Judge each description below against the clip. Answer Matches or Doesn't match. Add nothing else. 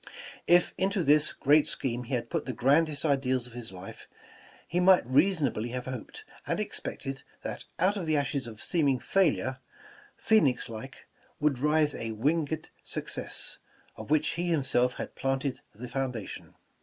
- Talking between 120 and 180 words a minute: Matches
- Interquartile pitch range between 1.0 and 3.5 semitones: Doesn't match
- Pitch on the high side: Doesn't match